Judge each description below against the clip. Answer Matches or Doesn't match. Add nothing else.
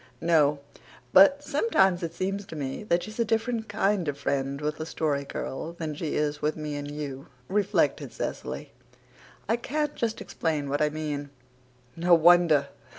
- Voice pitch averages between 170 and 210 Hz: Doesn't match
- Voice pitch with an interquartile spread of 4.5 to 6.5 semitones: Matches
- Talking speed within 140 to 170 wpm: Matches